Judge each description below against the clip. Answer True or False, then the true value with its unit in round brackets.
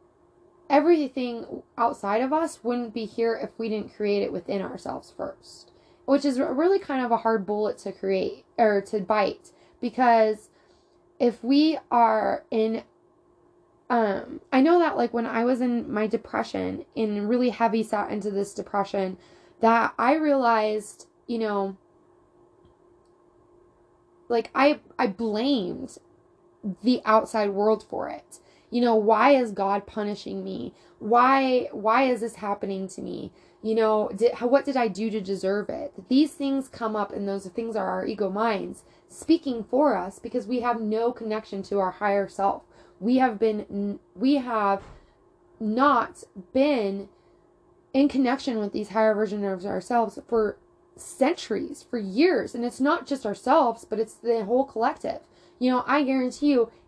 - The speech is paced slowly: False (155 wpm)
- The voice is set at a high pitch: True (235 Hz)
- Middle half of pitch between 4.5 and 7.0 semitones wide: True (5.1 semitones)